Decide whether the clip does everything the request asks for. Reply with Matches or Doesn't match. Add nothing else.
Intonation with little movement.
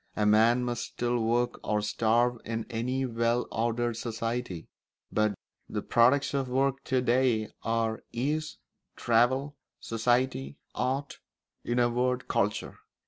Matches